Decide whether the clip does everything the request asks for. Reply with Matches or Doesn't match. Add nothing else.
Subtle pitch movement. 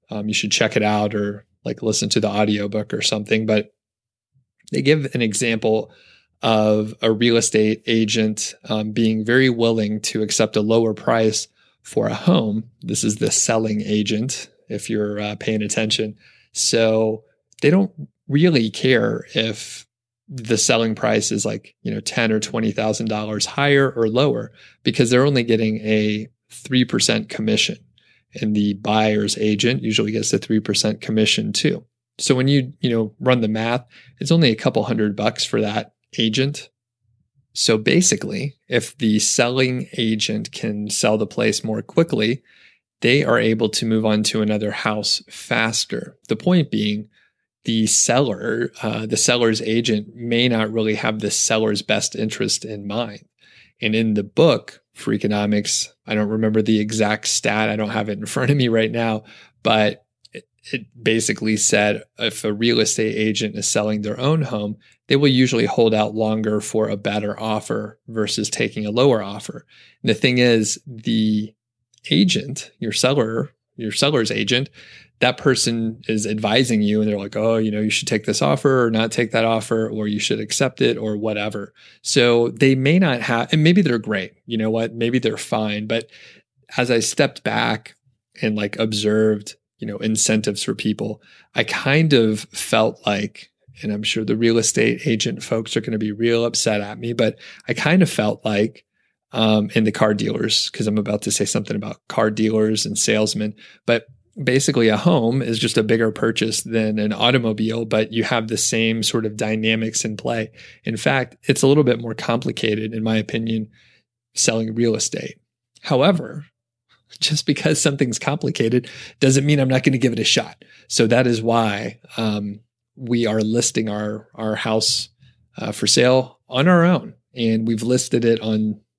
Matches